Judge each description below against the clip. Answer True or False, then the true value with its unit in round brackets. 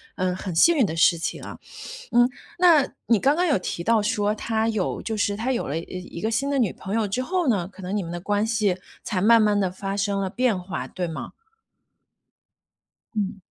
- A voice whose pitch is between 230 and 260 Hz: False (210 Hz)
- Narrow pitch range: False (3.8 semitones)